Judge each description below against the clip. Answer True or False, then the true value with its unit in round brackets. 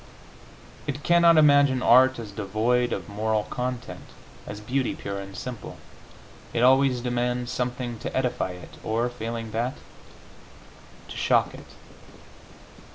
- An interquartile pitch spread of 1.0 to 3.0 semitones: True (2.7 semitones)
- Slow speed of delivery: True (125 wpm)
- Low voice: True (120 Hz)